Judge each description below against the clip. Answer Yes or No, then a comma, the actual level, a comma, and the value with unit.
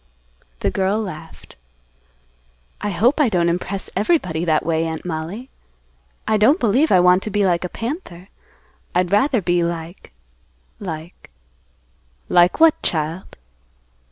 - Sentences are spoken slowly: Yes, slow, 130 wpm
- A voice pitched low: No, medium, 180 Hz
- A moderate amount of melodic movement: Yes, average, 4.3 semitones